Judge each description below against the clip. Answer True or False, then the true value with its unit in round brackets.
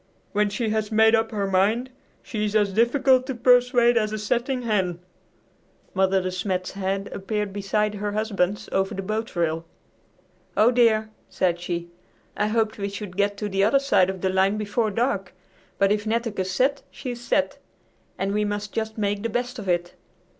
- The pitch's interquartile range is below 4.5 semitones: True (2.8 semitones)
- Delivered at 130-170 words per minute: False (180 wpm)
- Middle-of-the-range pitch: False (210 Hz)